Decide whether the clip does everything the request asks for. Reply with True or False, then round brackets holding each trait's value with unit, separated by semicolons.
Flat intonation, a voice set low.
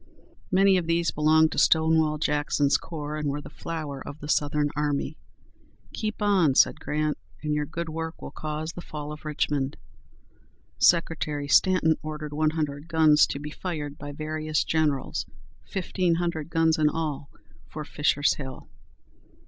False (1.7 semitones; 155 Hz)